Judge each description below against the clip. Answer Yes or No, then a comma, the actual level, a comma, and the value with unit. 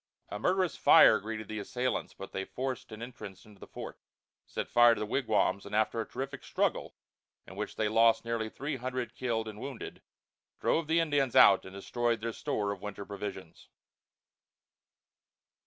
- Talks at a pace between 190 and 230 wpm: No, average, 170 wpm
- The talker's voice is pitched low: Yes, low, 110 Hz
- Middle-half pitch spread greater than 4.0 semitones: No, average, 3.7 semitones